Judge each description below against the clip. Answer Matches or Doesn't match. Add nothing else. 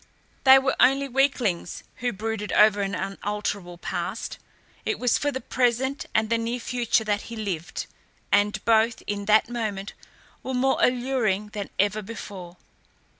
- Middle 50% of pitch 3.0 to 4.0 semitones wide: Matches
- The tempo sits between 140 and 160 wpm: Matches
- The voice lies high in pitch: Matches